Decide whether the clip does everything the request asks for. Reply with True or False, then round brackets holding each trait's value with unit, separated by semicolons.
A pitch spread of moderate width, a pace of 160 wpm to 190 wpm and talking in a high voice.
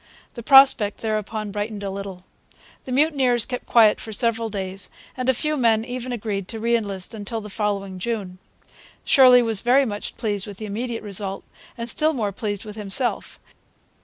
True (3.1 semitones; 175 wpm; 220 Hz)